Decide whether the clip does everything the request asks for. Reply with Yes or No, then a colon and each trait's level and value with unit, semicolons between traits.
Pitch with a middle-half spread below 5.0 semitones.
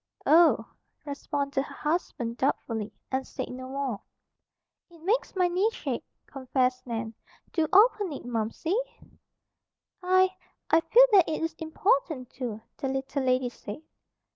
No: wide, 5.4 semitones